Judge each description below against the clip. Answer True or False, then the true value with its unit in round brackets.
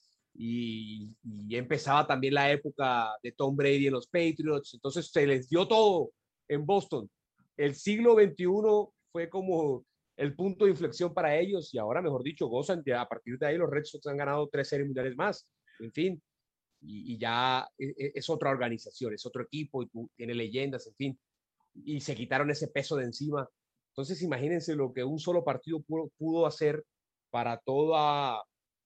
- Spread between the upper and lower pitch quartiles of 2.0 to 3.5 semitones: False (4.1 semitones)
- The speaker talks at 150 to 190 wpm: True (180 wpm)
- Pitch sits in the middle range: True (145 Hz)